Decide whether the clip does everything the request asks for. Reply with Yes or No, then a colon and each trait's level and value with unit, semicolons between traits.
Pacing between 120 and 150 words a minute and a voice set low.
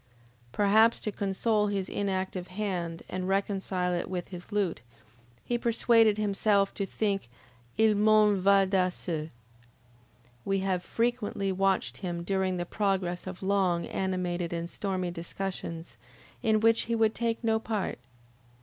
No: average, 140 wpm; high, 195 Hz